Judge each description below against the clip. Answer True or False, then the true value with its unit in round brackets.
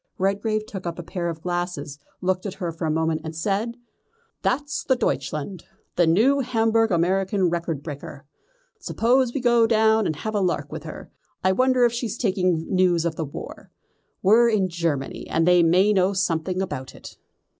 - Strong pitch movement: False (4.9 semitones)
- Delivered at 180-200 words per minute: True (185 wpm)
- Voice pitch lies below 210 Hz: True (185 Hz)